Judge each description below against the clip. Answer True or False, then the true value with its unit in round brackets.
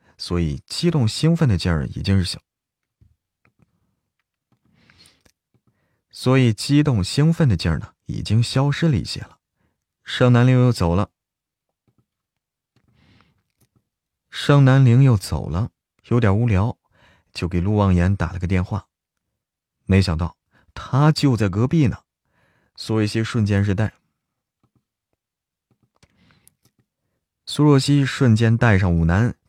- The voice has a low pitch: True (110 Hz)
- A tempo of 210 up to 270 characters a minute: False (165 characters per minute)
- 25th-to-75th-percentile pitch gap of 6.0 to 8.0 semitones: False (5.6 semitones)